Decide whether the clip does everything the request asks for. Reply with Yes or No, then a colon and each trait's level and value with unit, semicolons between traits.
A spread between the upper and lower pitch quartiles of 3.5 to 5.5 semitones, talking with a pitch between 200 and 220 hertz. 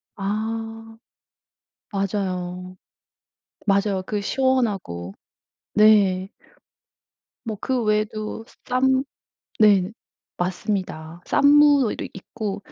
No: average, 3.0 semitones; high, 210 Hz